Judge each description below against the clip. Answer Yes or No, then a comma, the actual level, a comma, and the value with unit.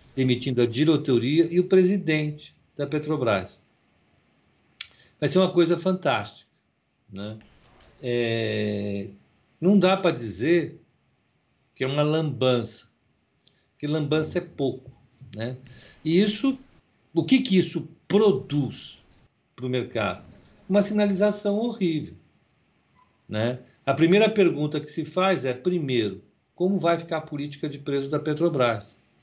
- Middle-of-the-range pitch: Yes, medium, 150 Hz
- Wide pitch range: Yes, wide, 6.0 semitones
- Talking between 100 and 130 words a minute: Yes, slow, 120 wpm